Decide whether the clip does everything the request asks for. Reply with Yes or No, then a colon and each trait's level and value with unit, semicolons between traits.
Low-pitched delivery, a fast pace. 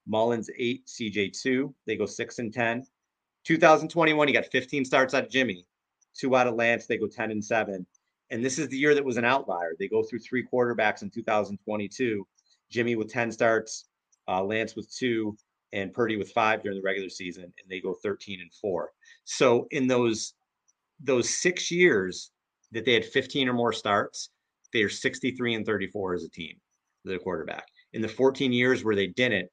No: low, 115 Hz; average, 185 wpm